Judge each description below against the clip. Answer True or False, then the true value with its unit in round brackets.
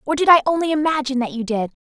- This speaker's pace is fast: True (265 wpm)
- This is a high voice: True (275 Hz)